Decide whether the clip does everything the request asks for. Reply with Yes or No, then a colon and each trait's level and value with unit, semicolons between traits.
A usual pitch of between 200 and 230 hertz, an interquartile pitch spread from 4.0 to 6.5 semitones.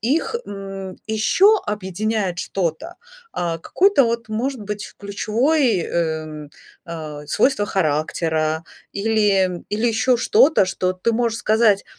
Yes: high, 205 Hz; average, 5.1 semitones